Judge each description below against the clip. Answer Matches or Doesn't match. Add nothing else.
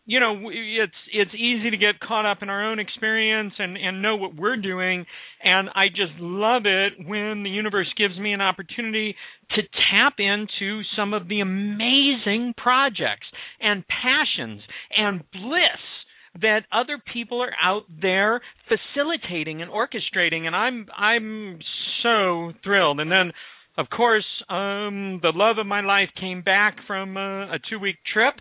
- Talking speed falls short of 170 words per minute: Matches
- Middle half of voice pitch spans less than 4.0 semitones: Matches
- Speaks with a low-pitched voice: Doesn't match